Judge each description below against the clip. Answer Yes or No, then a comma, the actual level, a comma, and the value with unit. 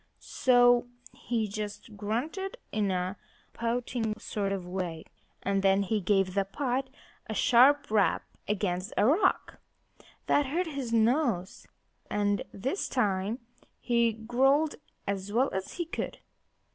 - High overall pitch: Yes, high, 220 Hz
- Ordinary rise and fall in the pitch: Yes, average, 4.6 semitones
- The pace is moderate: No, slow, 130 wpm